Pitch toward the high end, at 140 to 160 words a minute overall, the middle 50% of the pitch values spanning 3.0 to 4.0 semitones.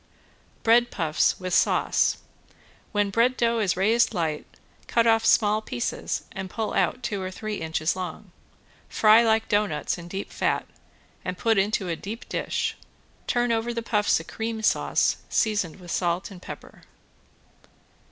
Yes: high, 210 Hz; average, 150 wpm; average, 3.7 semitones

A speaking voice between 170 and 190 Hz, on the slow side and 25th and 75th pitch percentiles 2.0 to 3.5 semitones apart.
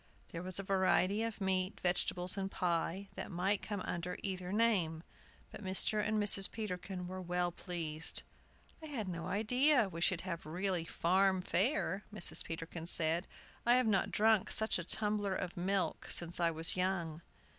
No: medium, 185 Hz; average, 165 wpm; average, 2.8 semitones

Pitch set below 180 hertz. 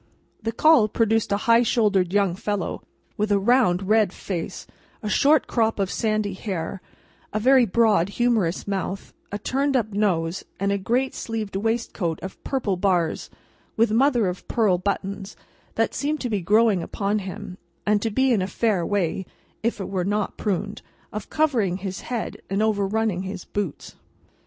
No: high, 205 Hz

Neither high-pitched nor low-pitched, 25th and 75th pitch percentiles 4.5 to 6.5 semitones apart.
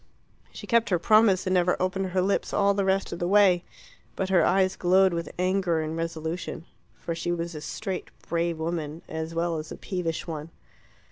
No: medium, 175 Hz; narrow, 2.4 semitones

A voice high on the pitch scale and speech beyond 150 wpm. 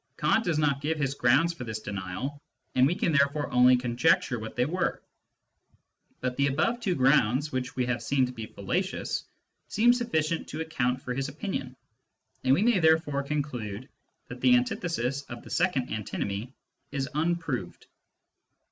No: low, 135 Hz; average, 165 wpm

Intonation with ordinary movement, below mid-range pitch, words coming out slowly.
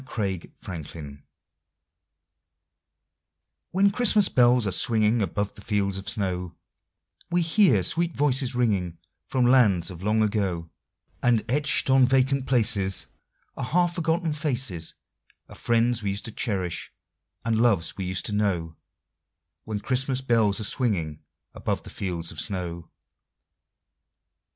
No: wide, 5.7 semitones; low, 110 Hz; slow, 130 wpm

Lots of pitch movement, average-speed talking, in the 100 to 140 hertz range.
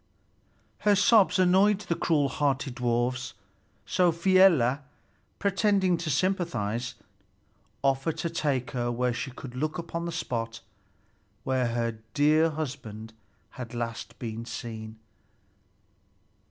No: wide, 6.1 semitones; slow, 115 wpm; low, 135 Hz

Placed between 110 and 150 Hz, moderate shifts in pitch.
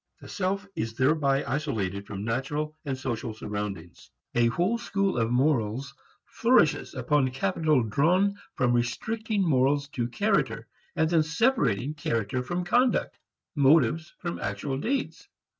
No: medium, 140 Hz; wide, 6.3 semitones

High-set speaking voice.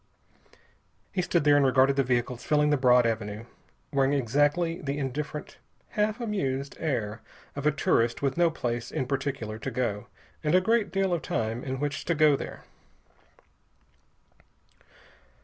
No: medium, 140 Hz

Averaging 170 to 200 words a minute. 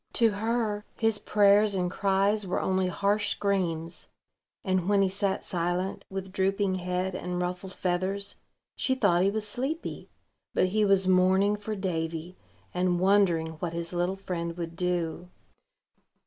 No: average, 150 wpm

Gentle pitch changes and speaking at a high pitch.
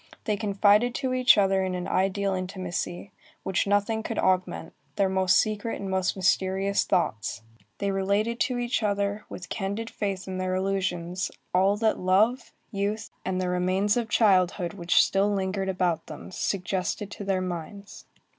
Yes: narrow, 1.9 semitones; high, 195 Hz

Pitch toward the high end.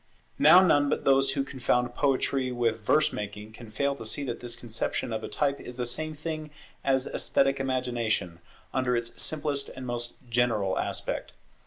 No: low, 125 Hz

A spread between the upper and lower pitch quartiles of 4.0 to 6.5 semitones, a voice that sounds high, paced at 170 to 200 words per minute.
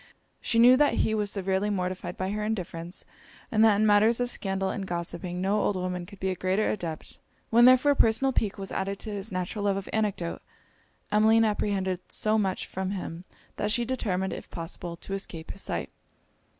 No: average, 2.7 semitones; high, 195 Hz; average, 190 wpm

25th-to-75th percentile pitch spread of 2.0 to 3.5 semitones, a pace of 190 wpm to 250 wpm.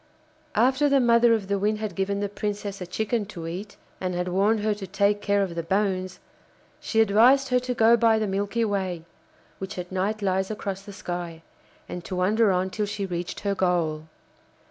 Yes: average, 2.7 semitones; average, 200 wpm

